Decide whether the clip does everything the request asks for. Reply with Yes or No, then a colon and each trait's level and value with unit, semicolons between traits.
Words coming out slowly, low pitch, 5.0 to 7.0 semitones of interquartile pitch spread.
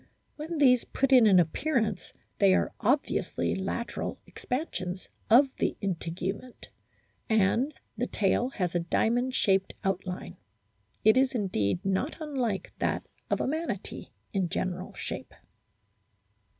No: slow, 125 wpm; high, 215 Hz; wide, 5.5 semitones